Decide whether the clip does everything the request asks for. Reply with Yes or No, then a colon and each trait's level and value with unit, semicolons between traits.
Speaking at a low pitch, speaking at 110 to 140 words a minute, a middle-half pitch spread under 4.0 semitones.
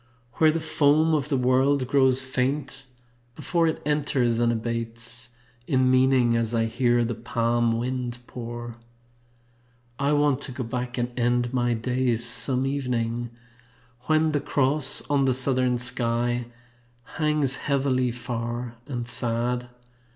Yes: low, 125 Hz; slow, 135 wpm; narrow, 2.4 semitones